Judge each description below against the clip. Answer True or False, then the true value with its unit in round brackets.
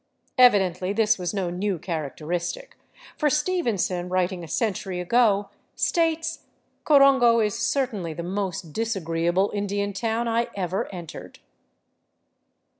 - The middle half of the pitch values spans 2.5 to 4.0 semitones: False (4.7 semitones)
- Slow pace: True (115 wpm)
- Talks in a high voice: True (200 Hz)